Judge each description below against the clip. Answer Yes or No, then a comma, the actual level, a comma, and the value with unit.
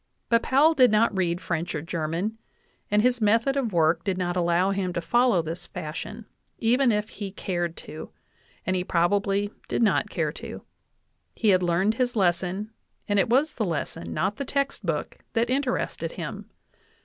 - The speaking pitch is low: No, high, 200 Hz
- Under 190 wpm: Yes, average, 180 wpm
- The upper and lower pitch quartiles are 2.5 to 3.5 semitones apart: No, average, 4.9 semitones